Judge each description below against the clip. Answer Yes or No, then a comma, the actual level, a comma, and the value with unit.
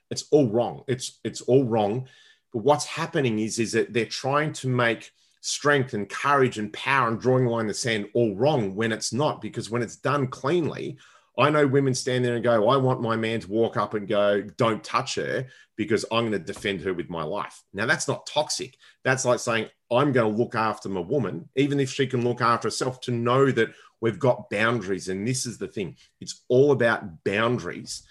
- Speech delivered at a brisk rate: Yes, fast, 215 wpm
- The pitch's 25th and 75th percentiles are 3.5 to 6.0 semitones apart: No, average, 2.9 semitones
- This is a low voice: Yes, low, 120 Hz